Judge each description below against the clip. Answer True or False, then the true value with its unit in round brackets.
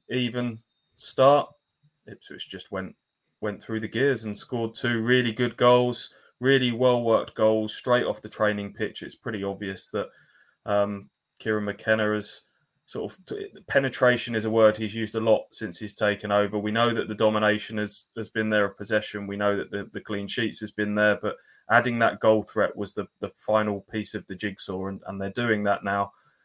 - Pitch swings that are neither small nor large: False (2.2 semitones)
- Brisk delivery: False (195 wpm)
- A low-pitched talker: True (110 Hz)